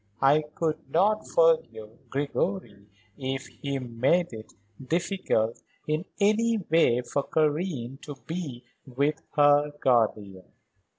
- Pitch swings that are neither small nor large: No, wide, 5.8 semitones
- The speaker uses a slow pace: Yes, slow, 110 wpm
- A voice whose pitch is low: No, medium, 145 Hz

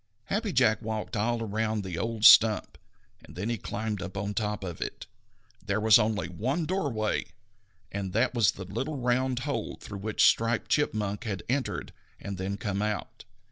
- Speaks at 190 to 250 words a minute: No, average, 175 wpm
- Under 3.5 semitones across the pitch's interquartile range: Yes, average, 2.8 semitones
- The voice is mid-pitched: No, low, 110 Hz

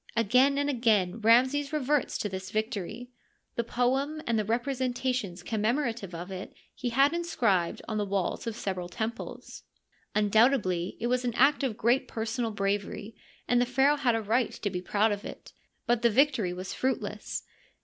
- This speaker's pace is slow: No, average, 170 wpm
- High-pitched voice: Yes, high, 230 Hz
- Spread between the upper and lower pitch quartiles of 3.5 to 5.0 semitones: Yes, average, 3.9 semitones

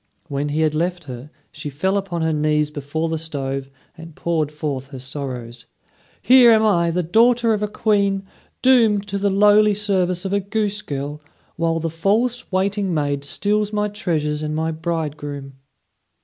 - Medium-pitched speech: Yes, medium, 165 Hz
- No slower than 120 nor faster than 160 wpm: No, average, 170 wpm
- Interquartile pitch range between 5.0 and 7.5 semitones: Yes, wide, 5.4 semitones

